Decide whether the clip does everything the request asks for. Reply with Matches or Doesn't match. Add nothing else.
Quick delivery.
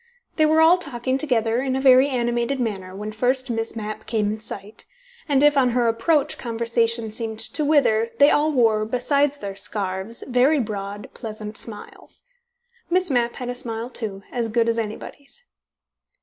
Doesn't match